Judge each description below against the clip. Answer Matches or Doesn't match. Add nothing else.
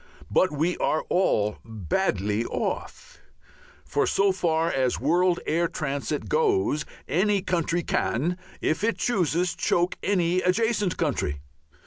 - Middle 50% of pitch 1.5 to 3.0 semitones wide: Doesn't match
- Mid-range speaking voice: Matches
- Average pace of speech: Doesn't match